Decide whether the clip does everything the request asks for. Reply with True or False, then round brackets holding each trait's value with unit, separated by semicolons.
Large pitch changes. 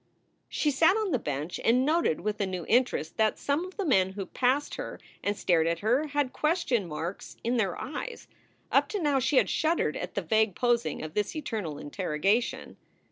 True (7.8 semitones)